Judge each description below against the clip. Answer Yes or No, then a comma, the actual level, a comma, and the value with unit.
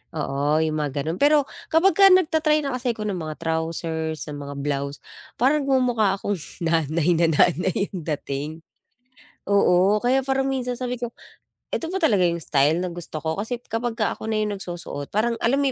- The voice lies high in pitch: Yes, high, 200 Hz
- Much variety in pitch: Yes, wide, 7.8 semitones